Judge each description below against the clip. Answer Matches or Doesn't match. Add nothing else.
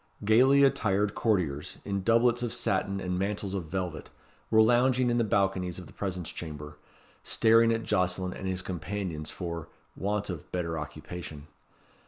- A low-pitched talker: Matches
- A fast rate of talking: Doesn't match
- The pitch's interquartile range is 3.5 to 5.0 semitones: Matches